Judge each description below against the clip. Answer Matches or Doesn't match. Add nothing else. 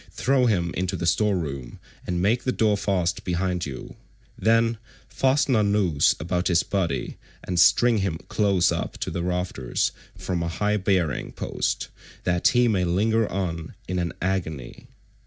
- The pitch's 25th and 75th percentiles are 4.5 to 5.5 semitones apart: Doesn't match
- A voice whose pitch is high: Doesn't match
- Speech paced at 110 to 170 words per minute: Matches